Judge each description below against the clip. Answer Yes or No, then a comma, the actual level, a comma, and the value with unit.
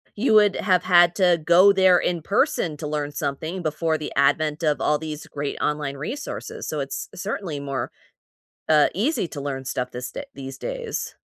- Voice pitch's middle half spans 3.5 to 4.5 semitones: Yes, average, 4.1 semitones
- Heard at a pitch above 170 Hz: No, medium, 155 Hz